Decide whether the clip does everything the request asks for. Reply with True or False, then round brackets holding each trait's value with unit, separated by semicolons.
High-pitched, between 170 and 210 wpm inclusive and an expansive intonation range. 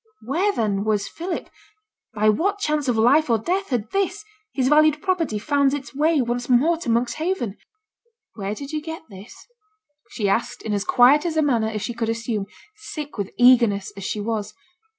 True (250 Hz; 180 wpm; 6.1 semitones)